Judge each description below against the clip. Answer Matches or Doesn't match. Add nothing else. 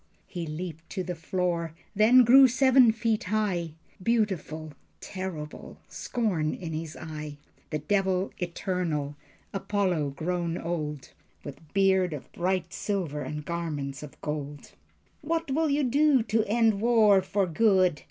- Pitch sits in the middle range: Matches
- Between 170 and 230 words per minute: Doesn't match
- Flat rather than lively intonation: Doesn't match